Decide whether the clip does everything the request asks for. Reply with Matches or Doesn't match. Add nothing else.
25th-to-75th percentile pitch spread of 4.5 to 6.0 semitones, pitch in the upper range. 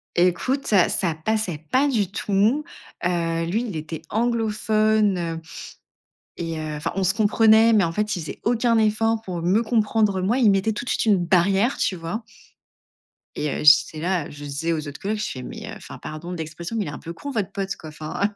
Matches